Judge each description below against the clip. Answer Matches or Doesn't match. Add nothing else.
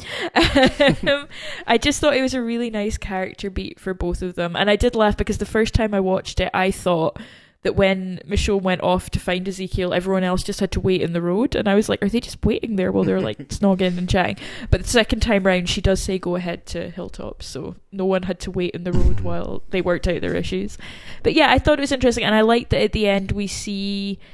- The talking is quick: Matches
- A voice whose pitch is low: Doesn't match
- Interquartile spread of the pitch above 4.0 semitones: Doesn't match